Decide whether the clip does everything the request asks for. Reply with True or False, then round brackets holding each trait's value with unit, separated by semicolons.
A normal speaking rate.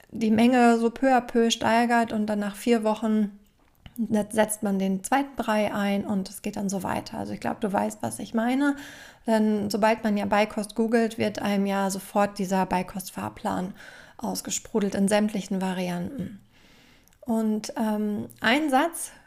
True (160 wpm)